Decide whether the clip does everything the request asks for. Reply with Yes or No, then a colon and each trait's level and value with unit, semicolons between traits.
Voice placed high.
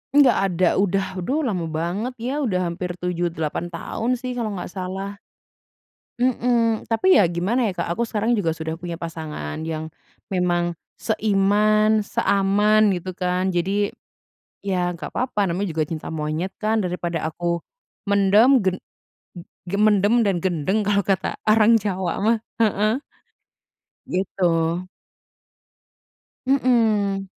Yes: high, 195 Hz